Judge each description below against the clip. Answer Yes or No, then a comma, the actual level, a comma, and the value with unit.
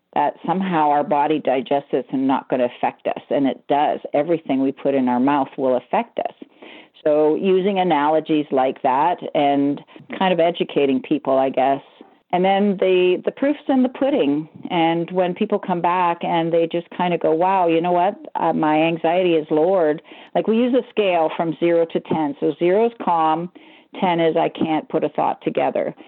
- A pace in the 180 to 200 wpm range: Yes, average, 195 wpm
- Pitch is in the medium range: Yes, medium, 170 Hz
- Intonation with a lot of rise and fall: No, average, 3.7 semitones